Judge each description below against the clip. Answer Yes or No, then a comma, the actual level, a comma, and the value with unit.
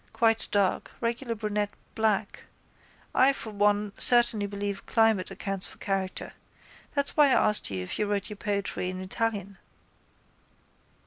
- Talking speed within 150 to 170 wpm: No, average, 140 wpm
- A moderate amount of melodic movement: No, narrow, 2.2 semitones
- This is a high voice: Yes, high, 205 Hz